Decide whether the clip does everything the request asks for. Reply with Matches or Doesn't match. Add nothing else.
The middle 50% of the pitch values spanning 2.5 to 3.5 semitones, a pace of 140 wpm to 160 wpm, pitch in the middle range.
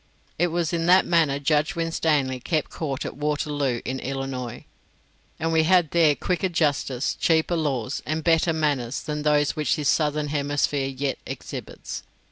Matches